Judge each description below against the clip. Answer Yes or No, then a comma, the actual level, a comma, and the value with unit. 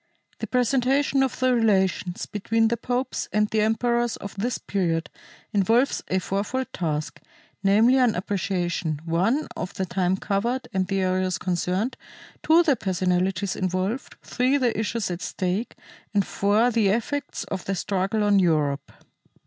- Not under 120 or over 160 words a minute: Yes, average, 150 wpm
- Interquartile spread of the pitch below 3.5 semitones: No, average, 4.4 semitones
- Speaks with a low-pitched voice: No, high, 200 Hz